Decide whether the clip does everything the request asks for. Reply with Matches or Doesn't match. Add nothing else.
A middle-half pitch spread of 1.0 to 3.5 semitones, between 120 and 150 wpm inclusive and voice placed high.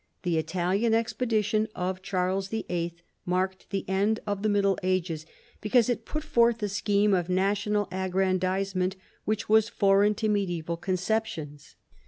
Matches